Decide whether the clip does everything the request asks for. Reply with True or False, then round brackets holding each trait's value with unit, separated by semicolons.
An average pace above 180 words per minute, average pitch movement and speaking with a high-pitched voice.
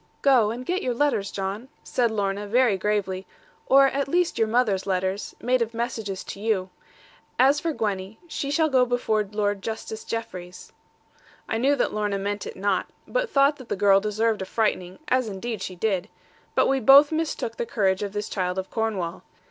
True (190 wpm; 4.5 semitones; 220 Hz)